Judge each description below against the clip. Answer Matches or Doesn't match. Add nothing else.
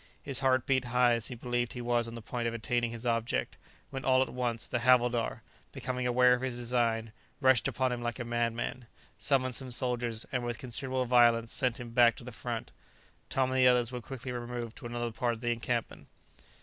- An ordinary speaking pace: Doesn't match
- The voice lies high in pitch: Doesn't match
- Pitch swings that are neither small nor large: Doesn't match